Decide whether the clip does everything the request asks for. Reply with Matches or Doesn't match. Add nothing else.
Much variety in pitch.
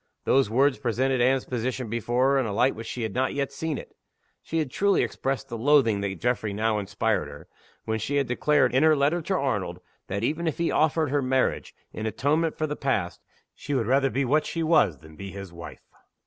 Doesn't match